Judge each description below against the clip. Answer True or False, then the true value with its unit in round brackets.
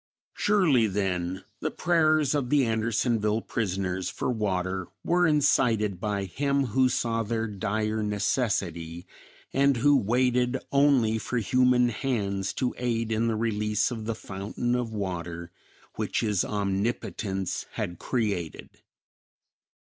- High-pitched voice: False (110 Hz)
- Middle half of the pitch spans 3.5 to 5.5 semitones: True (4.2 semitones)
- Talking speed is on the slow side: True (125 wpm)